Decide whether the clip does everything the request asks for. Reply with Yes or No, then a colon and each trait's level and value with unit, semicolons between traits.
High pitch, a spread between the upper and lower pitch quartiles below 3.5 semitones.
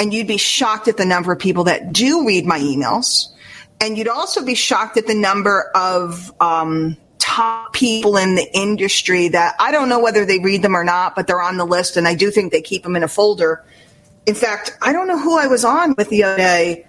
No: high, 195 Hz; average, 4.1 semitones